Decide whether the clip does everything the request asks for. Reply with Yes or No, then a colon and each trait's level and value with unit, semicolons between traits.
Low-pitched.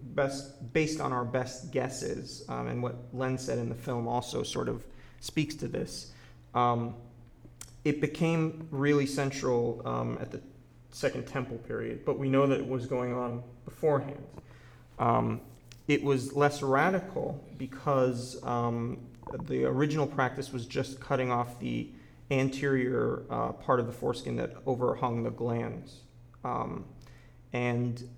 Yes: low, 125 Hz